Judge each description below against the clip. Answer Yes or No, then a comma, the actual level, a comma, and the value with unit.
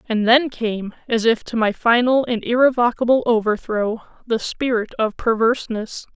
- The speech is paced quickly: No, average, 145 wpm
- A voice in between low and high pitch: No, high, 230 Hz